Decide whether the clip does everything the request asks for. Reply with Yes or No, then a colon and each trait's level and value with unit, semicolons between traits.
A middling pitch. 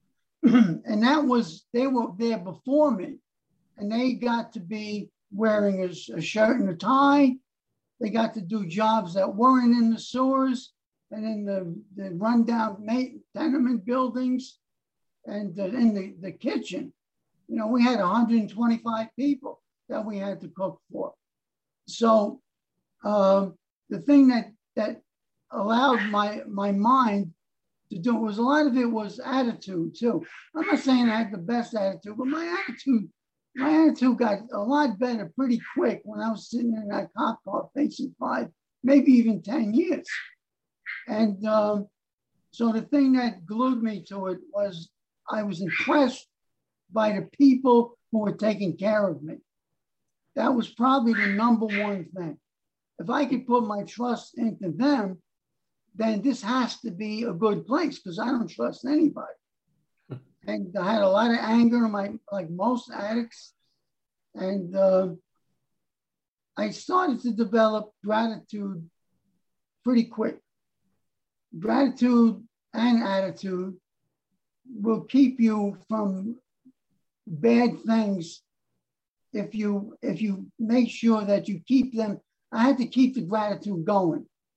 No: high, 225 Hz